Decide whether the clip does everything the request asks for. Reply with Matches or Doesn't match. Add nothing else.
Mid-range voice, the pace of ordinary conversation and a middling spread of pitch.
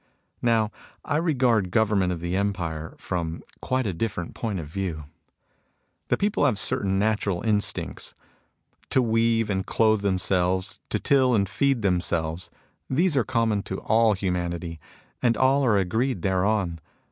Doesn't match